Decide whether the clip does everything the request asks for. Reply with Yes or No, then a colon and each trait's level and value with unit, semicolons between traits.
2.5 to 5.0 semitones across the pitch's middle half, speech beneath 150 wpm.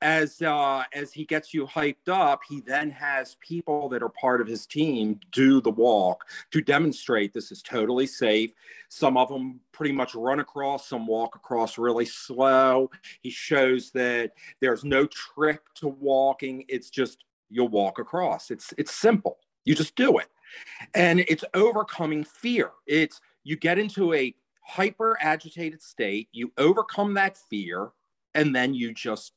No: average, 4.1 semitones; average, 160 wpm